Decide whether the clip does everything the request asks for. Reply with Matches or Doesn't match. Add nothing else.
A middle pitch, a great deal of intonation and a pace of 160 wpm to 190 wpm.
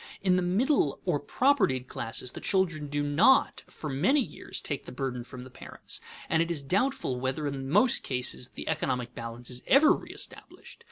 Matches